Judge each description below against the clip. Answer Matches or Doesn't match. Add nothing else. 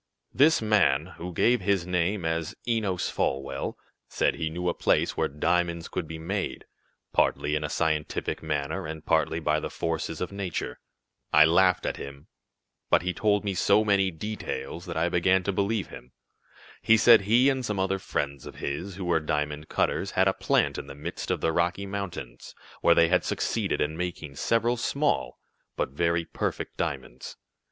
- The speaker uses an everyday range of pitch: Matches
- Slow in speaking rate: Doesn't match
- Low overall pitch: Matches